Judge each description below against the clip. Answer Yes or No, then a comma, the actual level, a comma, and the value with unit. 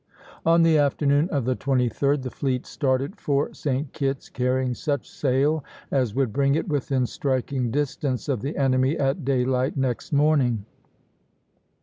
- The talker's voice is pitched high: No, low, 135 Hz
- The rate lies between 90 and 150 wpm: Yes, average, 145 wpm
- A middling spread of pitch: No, narrow, 2.0 semitones